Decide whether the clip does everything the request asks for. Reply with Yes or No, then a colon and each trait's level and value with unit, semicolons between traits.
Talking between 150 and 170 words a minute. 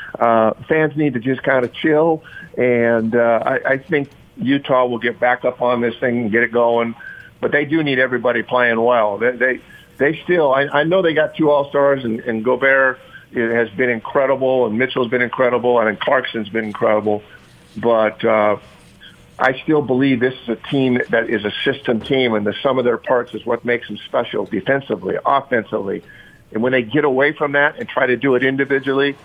No: average, 200 wpm